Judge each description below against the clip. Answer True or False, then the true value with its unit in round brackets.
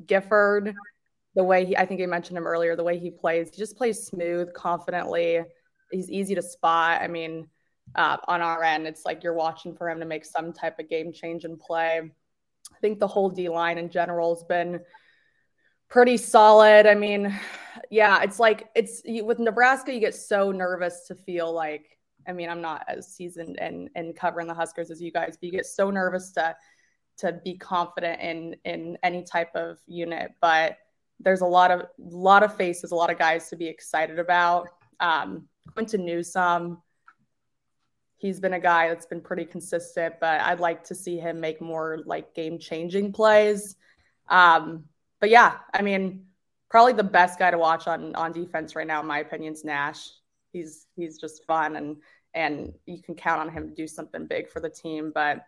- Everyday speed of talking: True (195 wpm)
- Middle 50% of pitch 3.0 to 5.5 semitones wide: False (2.5 semitones)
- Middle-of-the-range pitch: True (175 Hz)